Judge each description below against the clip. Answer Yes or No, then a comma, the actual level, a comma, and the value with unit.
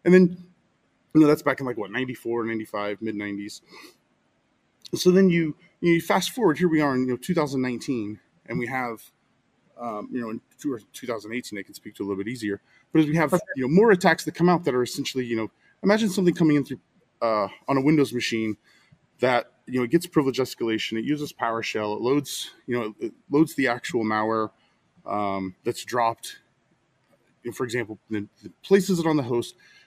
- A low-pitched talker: Yes, low, 130 Hz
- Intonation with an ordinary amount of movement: No, wide, 6.6 semitones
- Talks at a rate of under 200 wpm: No, fast, 205 wpm